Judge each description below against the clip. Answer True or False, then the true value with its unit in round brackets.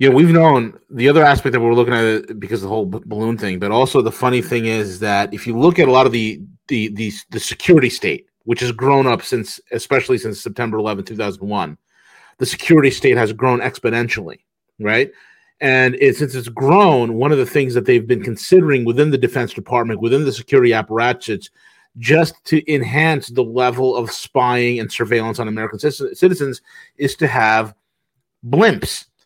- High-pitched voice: False (125 Hz)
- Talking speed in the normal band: True (190 wpm)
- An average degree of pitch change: True (3.7 semitones)